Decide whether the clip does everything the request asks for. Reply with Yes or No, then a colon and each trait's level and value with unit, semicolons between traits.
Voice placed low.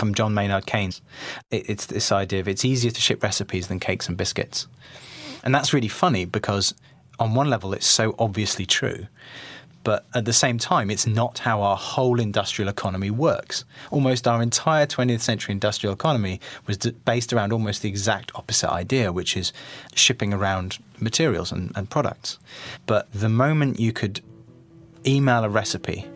Yes: low, 110 Hz